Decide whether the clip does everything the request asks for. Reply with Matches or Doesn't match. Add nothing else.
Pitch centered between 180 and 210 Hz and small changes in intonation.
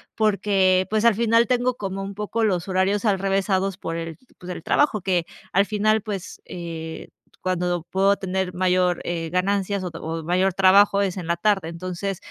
Matches